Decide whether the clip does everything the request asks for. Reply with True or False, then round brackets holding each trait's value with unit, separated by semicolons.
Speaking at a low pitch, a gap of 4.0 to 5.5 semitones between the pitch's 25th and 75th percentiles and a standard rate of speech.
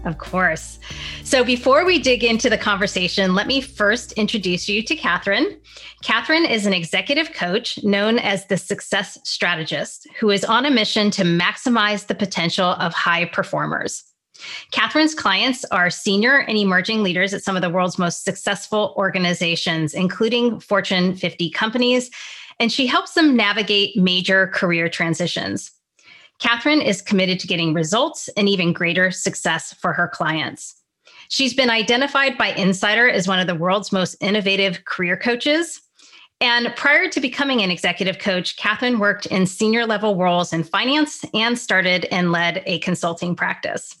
False (200 Hz; 4.7 semitones; 155 wpm)